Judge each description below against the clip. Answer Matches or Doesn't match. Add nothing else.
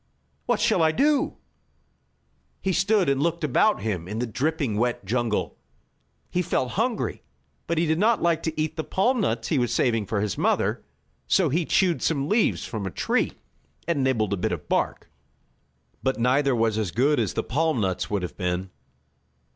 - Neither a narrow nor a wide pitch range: Doesn't match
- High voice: Doesn't match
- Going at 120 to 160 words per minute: Doesn't match